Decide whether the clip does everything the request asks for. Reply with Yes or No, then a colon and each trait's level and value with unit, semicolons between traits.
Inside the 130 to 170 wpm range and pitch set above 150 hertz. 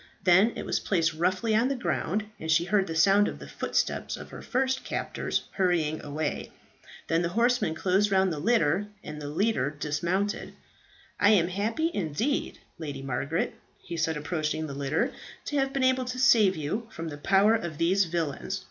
No: average, 185 wpm; medium, 185 Hz